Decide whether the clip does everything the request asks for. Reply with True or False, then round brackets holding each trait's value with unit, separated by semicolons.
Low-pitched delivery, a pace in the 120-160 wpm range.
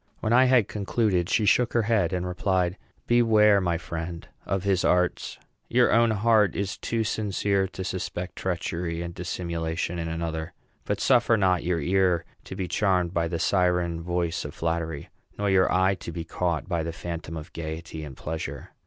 False (90 Hz; 180 wpm)